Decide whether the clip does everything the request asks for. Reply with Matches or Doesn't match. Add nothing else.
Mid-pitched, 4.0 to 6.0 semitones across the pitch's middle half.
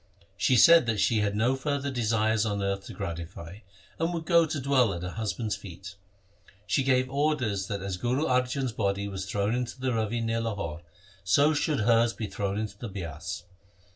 Doesn't match